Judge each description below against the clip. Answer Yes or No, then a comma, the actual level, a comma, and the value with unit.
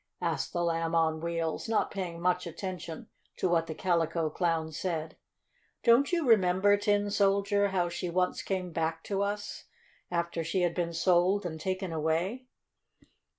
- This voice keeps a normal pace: Yes, average, 155 wpm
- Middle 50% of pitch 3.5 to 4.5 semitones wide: No, average, 3.1 semitones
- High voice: No, medium, 175 Hz